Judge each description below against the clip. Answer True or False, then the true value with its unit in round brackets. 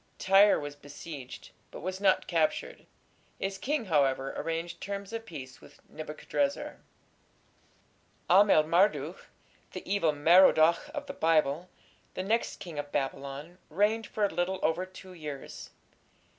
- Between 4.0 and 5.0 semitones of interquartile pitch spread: True (4.7 semitones)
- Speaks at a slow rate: True (130 wpm)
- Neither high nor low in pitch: True (170 Hz)